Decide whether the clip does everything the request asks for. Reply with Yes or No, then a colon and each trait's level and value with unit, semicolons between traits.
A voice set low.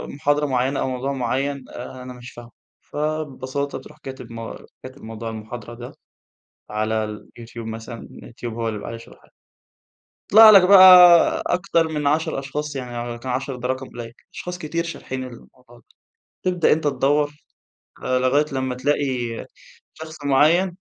Yes: low, 130 Hz